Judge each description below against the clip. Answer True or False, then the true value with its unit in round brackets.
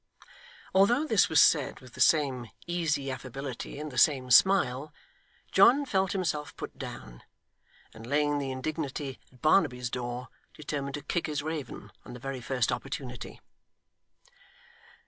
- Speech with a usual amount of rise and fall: True (3.6 semitones)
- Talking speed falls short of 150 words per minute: True (140 wpm)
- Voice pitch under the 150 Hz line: True (140 Hz)